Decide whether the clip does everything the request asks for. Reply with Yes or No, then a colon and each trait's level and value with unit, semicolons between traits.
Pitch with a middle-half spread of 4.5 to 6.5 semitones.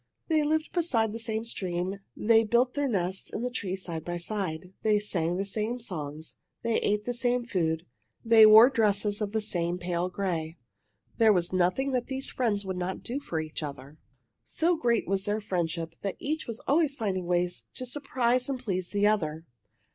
Yes: average, 5.1 semitones